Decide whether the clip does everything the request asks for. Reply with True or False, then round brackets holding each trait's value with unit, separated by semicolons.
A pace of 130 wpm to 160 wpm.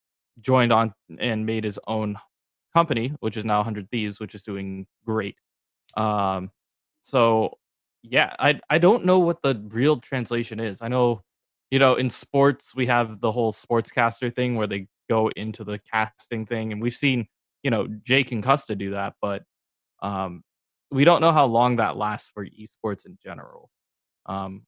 False (175 wpm)